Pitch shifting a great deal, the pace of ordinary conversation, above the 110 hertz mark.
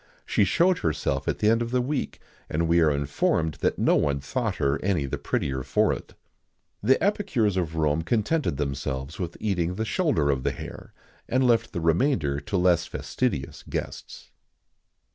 No: wide, 8.0 semitones; average, 180 wpm; very low, 85 Hz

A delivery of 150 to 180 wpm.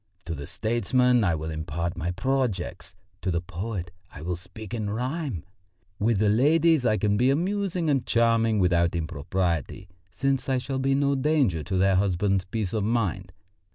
Yes: average, 170 wpm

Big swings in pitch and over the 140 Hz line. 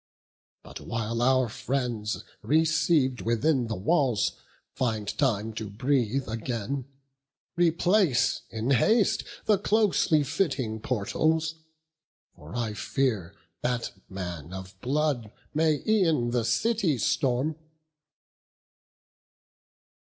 No: wide, 5.8 semitones; low, 125 Hz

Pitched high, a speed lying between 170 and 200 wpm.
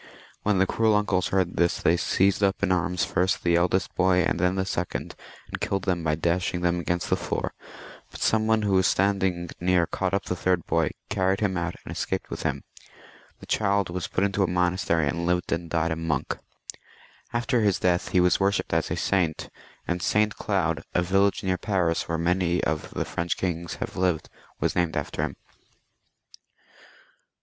No: very low, 90 Hz; average, 195 wpm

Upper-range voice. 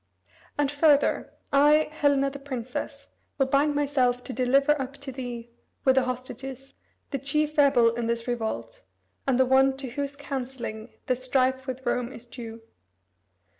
Yes: very high, 265 Hz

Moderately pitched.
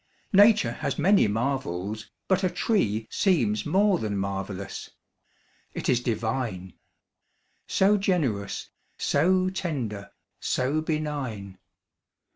No: low, 130 Hz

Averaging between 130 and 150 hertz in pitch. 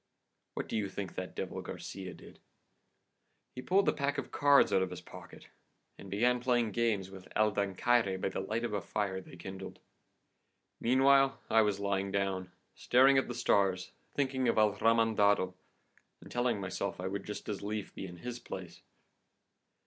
No: low, 105 Hz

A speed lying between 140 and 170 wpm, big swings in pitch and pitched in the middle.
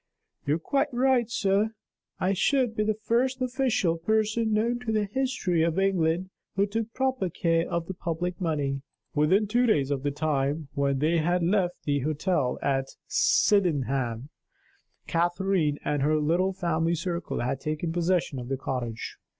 Yes: average, 160 wpm; wide, 6.0 semitones; medium, 175 Hz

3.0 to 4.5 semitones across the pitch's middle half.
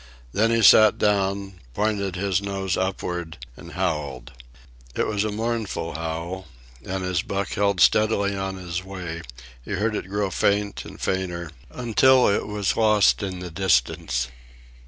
No: narrow, 2.5 semitones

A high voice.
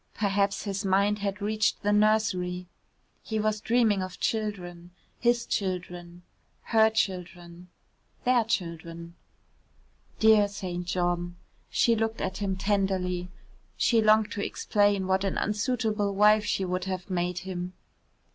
Yes: high, 200 Hz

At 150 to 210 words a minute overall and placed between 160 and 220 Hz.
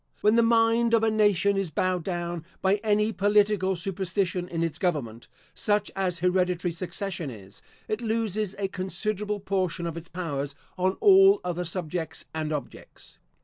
Yes: average, 155 wpm; medium, 185 Hz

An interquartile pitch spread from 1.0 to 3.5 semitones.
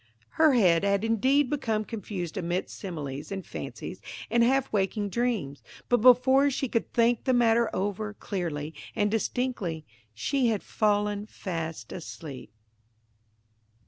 No: average, 5.1 semitones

